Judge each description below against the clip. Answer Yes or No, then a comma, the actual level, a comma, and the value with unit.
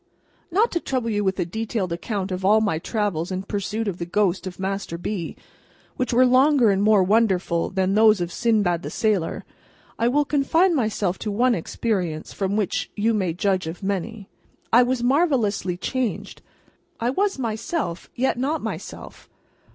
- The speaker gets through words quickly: No, average, 170 wpm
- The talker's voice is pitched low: No, high, 210 Hz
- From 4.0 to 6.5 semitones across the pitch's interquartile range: Yes, average, 4.5 semitones